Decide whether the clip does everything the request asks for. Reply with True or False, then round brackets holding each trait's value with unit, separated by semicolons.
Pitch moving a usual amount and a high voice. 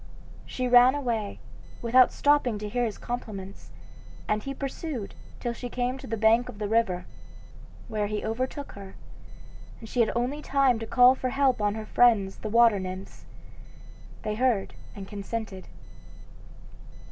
True (3.2 semitones; 230 Hz)